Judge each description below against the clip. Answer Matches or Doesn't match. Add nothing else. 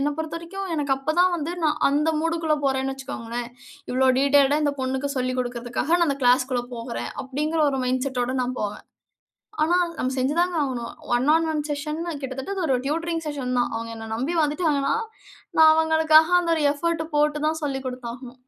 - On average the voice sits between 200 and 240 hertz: Doesn't match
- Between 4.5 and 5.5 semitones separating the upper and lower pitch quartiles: Doesn't match